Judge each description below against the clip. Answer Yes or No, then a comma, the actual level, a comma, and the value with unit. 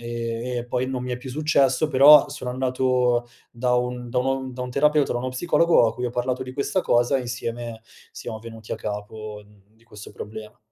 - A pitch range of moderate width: No, narrow, 2.0 semitones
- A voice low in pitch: Yes, low, 125 Hz